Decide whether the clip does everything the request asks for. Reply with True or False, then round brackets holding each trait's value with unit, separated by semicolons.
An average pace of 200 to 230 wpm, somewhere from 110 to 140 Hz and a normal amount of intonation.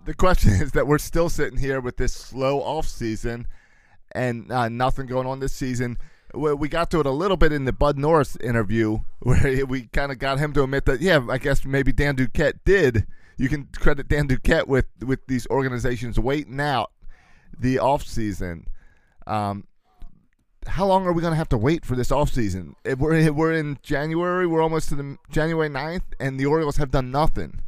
True (205 wpm; 135 Hz; 3.7 semitones)